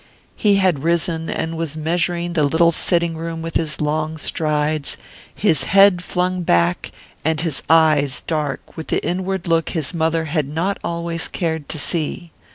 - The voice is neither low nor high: Yes, medium, 165 Hz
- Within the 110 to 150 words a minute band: No, average, 165 wpm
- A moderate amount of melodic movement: No, narrow, 1.9 semitones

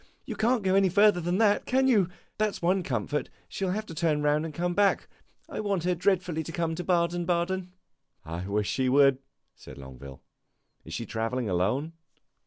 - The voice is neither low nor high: Yes, medium, 170 Hz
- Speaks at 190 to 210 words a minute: Yes, average, 195 wpm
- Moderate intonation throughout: No, wide, 6.3 semitones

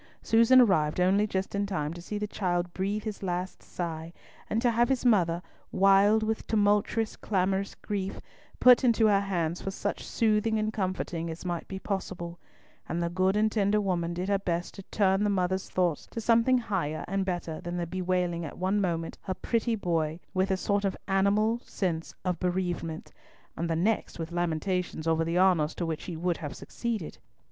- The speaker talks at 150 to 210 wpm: Yes, average, 190 wpm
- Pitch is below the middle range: No, high, 190 Hz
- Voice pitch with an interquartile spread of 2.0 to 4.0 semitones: Yes, average, 3.2 semitones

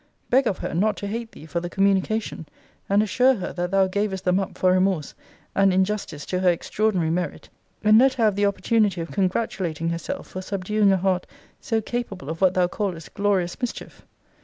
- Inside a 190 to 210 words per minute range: Yes, average, 200 wpm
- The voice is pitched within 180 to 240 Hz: Yes, high, 190 Hz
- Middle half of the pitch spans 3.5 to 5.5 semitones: No, average, 2.9 semitones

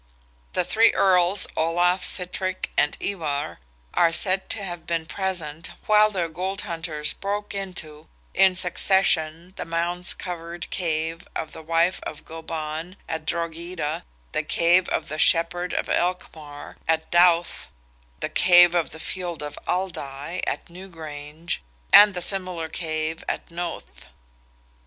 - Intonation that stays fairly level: Yes, narrow, 2.3 semitones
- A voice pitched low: No, medium, 170 Hz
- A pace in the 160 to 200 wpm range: No, average, 140 wpm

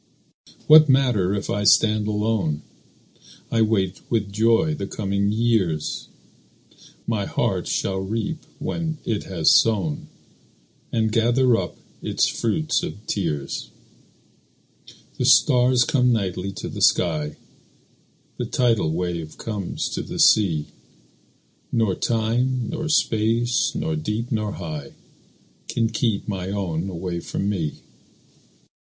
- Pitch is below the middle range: Yes, low, 105 Hz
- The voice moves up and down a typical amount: Yes, average, 3.9 semitones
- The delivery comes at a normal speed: No, slow, 120 wpm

